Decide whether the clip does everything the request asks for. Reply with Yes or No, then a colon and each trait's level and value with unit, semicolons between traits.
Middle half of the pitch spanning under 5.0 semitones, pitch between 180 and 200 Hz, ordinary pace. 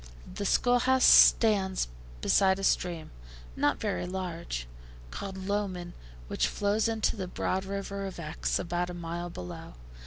Yes: narrow, 2.6 semitones; high, 190 Hz; average, 145 wpm